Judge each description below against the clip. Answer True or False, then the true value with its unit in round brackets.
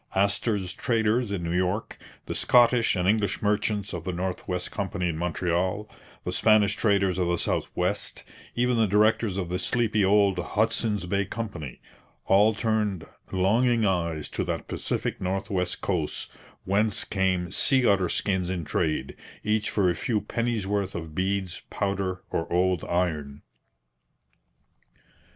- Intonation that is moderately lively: True (3.0 semitones)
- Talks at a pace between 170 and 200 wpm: False (150 wpm)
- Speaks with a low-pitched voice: True (95 Hz)